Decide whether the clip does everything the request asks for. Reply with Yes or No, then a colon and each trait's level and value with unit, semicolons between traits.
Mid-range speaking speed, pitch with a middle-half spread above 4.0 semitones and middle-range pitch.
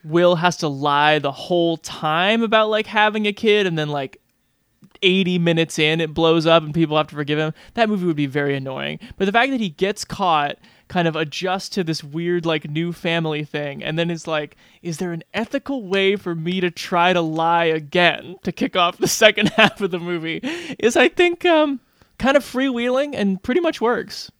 No: fast, 210 wpm; average, 4.8 semitones; medium, 175 Hz